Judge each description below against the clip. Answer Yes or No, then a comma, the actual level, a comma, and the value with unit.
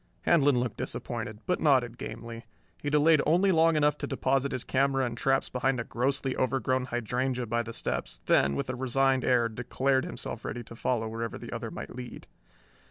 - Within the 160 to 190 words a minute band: Yes, average, 185 wpm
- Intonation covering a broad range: No, narrow, 2.5 semitones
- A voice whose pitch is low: Yes, low, 130 Hz